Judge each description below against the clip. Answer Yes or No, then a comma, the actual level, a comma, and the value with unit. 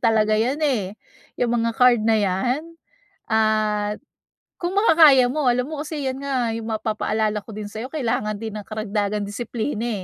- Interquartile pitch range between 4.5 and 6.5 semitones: No, average, 3.1 semitones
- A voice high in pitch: Yes, high, 225 Hz